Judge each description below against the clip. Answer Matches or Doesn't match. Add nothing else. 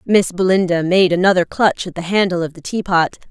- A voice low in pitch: Doesn't match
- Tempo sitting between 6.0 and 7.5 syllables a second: Doesn't match